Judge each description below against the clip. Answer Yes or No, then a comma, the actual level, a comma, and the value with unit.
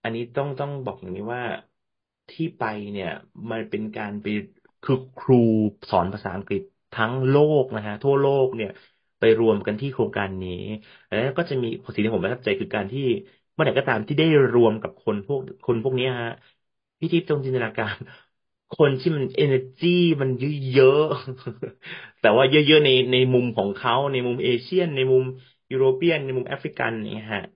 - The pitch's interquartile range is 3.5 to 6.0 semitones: Yes, average, 4.0 semitones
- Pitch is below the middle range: Yes, low, 130 Hz